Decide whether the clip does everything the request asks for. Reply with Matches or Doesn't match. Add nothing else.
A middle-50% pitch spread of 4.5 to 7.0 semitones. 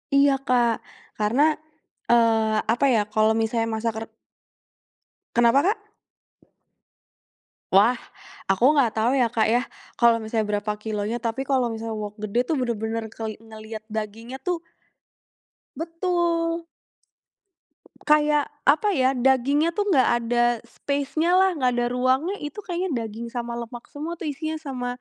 Matches